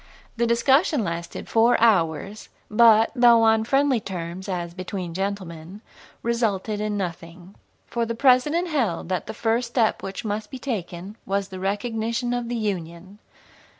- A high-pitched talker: Yes, high, 210 Hz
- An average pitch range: Yes, average, 4.1 semitones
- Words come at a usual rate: Yes, average, 150 wpm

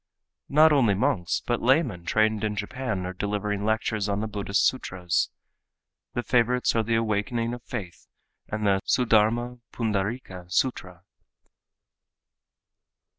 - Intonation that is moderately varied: Yes, average, 3.3 semitones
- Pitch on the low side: Yes, low, 110 Hz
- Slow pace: Yes, slow, 125 wpm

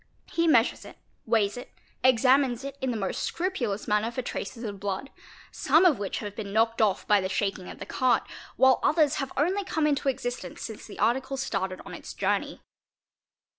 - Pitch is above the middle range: Yes, high, 245 Hz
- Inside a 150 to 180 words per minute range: No, average, 190 wpm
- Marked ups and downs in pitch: No, average, 4.8 semitones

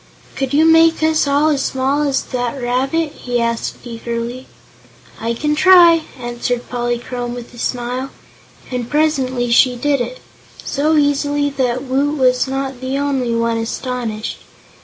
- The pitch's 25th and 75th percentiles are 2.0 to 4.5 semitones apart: Yes, average, 3.0 semitones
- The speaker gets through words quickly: No, average, 145 wpm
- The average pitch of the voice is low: No, very high, 260 Hz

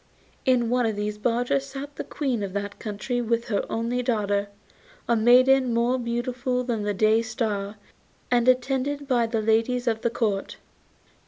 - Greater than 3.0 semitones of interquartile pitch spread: No, narrow, 2.5 semitones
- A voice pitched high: Yes, high, 235 Hz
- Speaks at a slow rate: No, average, 165 wpm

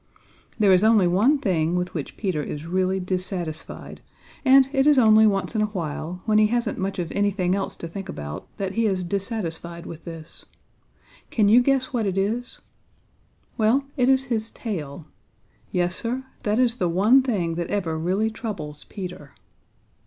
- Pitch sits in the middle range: No, high, 195 Hz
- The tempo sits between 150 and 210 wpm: Yes, average, 175 wpm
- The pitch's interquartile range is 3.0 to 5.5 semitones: Yes, average, 4.5 semitones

